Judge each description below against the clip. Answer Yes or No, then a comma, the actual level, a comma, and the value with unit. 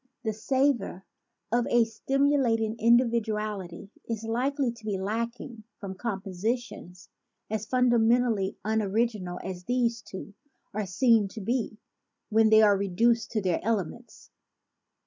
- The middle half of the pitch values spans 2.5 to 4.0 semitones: Yes, average, 3.0 semitones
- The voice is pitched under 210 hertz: No, high, 225 Hz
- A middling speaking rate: No, slow, 125 wpm